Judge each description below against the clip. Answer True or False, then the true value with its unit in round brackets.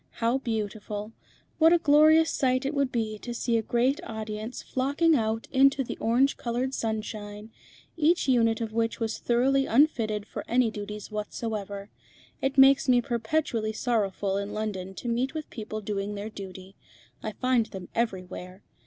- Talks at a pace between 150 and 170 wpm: True (160 wpm)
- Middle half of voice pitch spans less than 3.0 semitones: False (3.7 semitones)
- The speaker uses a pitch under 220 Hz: False (230 Hz)